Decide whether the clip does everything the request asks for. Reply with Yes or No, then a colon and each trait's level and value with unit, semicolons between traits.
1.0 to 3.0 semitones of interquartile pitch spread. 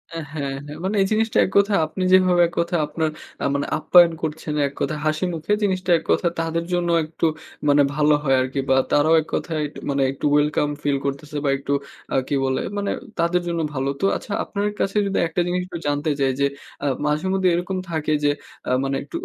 No: average, 3.7 semitones